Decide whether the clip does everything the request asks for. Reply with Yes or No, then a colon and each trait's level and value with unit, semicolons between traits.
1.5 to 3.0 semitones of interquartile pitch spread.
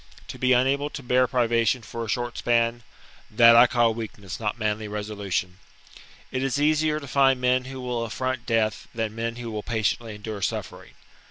Yes: average, 2.7 semitones